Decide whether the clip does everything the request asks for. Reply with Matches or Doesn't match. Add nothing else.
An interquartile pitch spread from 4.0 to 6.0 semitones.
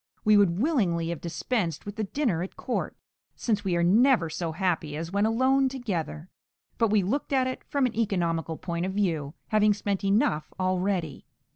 Matches